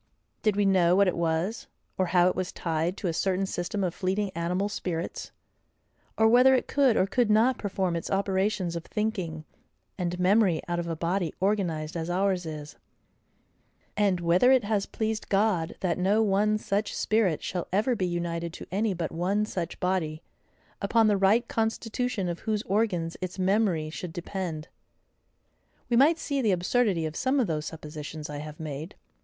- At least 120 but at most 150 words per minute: No, average, 175 wpm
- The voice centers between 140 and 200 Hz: Yes, medium, 185 Hz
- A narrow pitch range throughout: No, average, 3.9 semitones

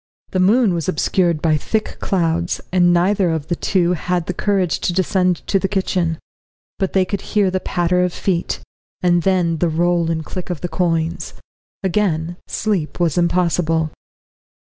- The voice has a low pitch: No, medium, 175 Hz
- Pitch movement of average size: No, narrow, 2.0 semitones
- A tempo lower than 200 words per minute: Yes, average, 165 wpm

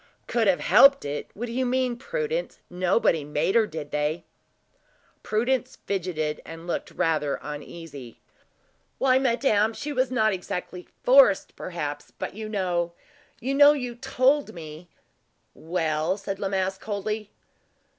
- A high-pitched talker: Yes, high, 195 Hz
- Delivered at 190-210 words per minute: No, average, 140 wpm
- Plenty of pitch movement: Yes, wide, 7.1 semitones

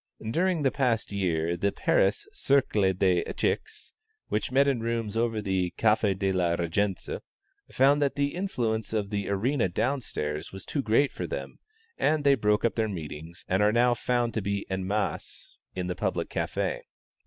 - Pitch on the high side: No, low, 105 Hz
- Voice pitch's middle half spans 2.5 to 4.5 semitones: No, average, 5.1 semitones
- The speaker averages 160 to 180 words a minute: Yes, average, 175 wpm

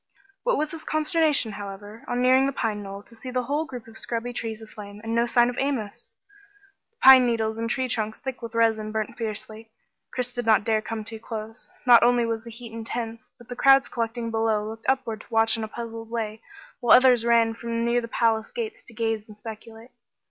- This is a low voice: No, high, 230 Hz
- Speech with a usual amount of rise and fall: No, narrow, 1.9 semitones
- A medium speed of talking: No, fast, 220 wpm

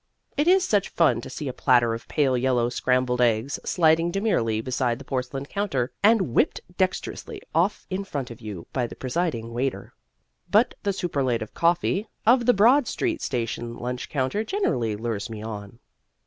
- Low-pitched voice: Yes, low, 130 Hz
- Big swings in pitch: Yes, wide, 8.1 semitones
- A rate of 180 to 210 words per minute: No, average, 170 wpm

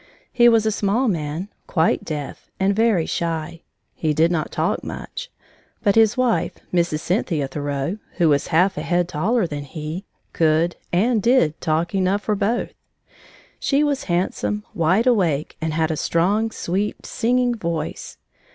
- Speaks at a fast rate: No, average, 155 wpm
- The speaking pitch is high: No, medium, 175 Hz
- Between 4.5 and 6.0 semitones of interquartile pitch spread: Yes, wide, 5.4 semitones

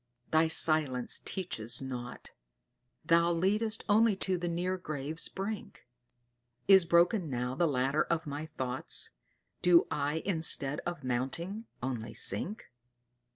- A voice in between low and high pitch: Yes, medium, 160 Hz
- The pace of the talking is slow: Yes, slow, 120 wpm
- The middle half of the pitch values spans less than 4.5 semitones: No, wide, 5.5 semitones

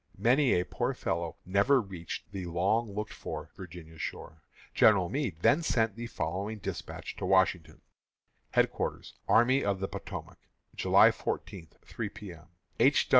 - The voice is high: No, low, 100 Hz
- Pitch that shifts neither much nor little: Yes, average, 4.6 semitones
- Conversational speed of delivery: Yes, average, 145 wpm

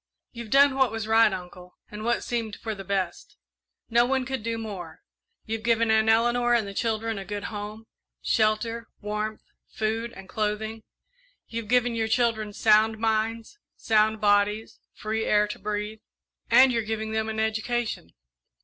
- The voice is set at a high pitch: Yes, high, 220 Hz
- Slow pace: No, average, 160 wpm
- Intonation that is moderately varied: No, narrow, 1.5 semitones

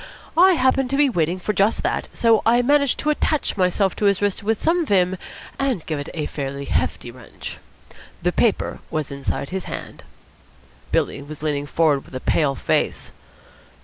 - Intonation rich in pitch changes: Yes, wide, 8.7 semitones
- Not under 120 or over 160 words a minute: No, average, 180 wpm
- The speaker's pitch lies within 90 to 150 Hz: No, high, 190 Hz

